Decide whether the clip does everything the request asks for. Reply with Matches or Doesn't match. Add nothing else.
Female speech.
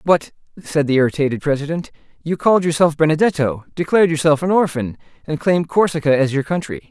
Doesn't match